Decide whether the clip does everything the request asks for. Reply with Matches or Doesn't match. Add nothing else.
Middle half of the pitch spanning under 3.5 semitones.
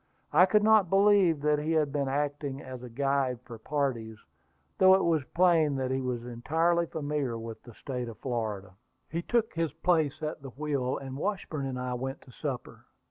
Doesn't match